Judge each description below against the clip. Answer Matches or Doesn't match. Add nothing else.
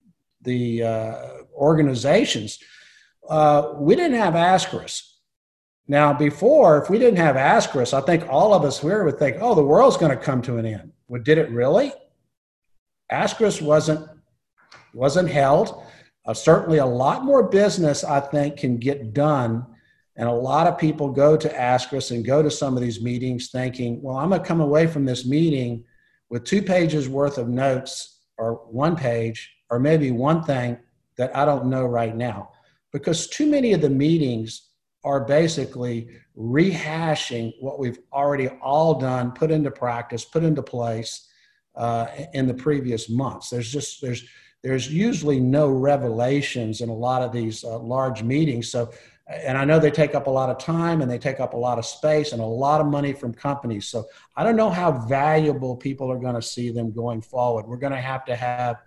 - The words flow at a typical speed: Matches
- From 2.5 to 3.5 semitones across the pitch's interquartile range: Doesn't match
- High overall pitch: Doesn't match